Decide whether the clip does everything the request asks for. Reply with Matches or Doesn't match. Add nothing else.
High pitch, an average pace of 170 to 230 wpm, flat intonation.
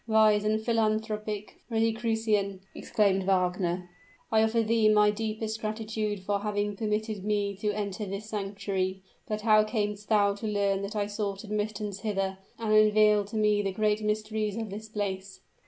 Doesn't match